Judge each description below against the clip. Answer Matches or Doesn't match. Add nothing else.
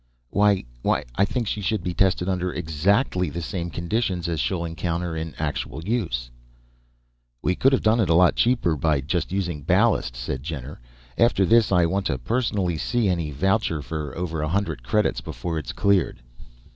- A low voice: Matches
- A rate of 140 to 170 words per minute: Doesn't match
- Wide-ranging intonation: Doesn't match